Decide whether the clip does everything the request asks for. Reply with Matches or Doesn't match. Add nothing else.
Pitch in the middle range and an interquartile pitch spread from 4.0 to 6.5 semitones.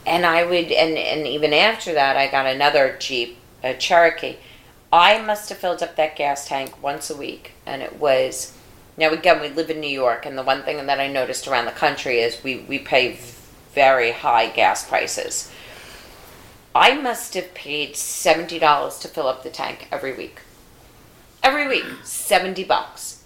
Matches